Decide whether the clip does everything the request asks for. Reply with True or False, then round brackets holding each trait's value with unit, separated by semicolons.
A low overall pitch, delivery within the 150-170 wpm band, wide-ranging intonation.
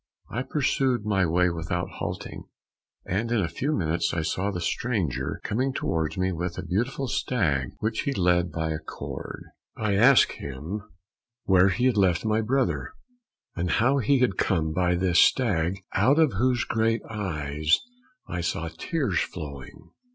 True (95 Hz; 160 wpm; 5.9 semitones)